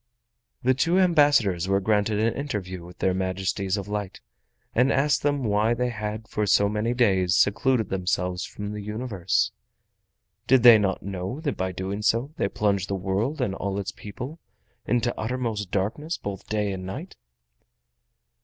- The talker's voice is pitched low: Yes, low, 105 Hz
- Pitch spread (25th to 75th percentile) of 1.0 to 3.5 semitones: No, average, 4.2 semitones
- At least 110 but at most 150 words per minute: No, average, 165 wpm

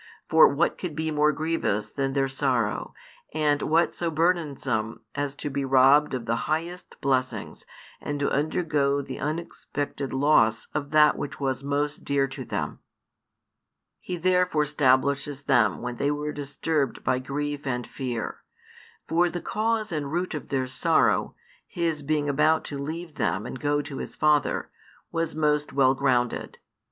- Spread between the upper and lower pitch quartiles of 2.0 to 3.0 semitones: Yes, narrow, 2.5 semitones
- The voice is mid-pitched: Yes, medium, 145 Hz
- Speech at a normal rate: Yes, average, 155 wpm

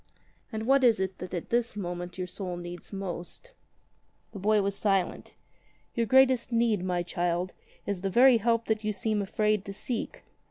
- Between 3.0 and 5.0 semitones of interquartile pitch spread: Yes, average, 4.1 semitones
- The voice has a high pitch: Yes, high, 200 Hz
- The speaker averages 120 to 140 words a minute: No, average, 185 wpm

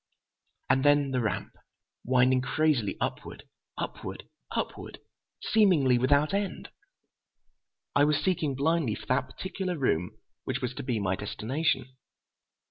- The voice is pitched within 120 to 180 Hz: Yes, low, 135 Hz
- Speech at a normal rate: No, slow, 115 wpm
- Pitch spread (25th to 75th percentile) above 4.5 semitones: No, average, 3.8 semitones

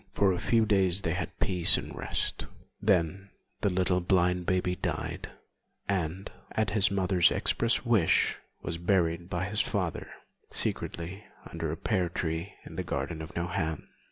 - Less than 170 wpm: Yes, average, 155 wpm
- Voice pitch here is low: Yes, very low, 90 Hz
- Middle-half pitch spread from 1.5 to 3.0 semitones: Yes, narrow, 2.5 semitones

